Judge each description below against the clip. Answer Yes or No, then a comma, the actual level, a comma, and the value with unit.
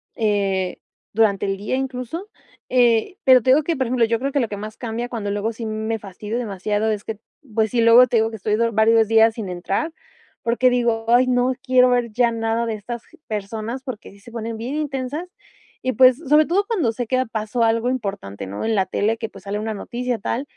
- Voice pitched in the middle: No, high, 230 Hz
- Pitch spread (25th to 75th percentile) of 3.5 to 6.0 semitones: No, average, 2.8 semitones